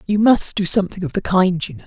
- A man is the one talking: No, female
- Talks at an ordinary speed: No, fast, 290 wpm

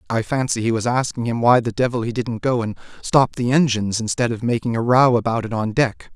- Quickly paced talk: Yes, fast, 245 wpm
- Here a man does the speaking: Yes, male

